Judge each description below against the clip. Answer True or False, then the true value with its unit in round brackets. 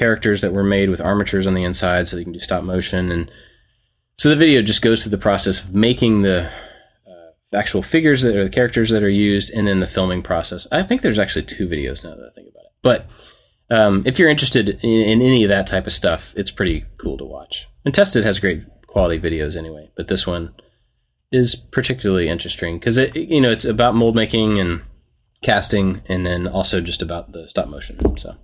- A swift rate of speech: True (220 wpm)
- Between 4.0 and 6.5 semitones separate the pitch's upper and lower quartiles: True (4.4 semitones)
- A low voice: True (100 Hz)